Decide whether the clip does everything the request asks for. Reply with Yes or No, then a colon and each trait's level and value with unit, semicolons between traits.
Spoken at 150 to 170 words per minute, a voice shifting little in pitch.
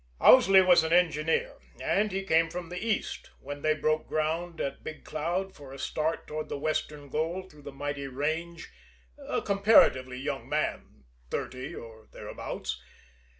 No: average, 155 wpm; average, 3.8 semitones